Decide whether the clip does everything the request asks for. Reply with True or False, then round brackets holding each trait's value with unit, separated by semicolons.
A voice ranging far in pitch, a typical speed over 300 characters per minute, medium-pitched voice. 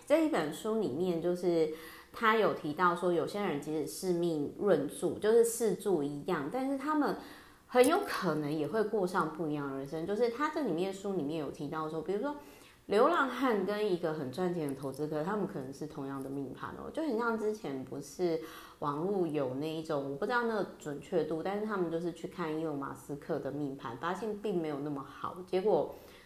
True (5.7 semitones; 310 characters per minute; 170 Hz)